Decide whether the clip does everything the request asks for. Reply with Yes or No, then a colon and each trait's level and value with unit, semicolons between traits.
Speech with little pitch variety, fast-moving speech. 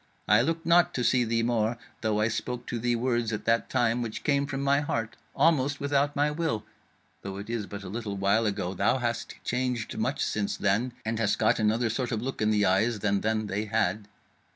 No: average, 3.1 semitones; fast, 220 wpm